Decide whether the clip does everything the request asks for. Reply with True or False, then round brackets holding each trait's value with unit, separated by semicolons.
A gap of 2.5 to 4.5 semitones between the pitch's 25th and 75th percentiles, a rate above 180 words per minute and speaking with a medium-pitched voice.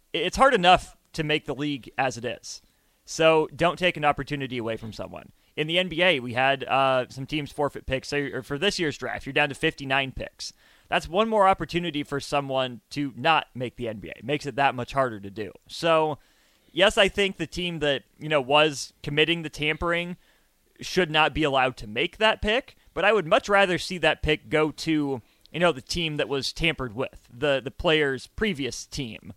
True (3.8 semitones; 205 wpm; 145 Hz)